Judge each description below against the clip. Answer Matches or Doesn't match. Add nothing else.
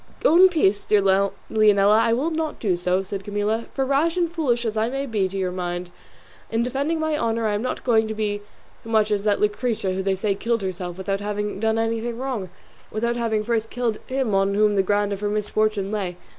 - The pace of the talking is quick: Matches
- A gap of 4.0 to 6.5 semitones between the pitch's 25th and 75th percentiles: Doesn't match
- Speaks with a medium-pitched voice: Doesn't match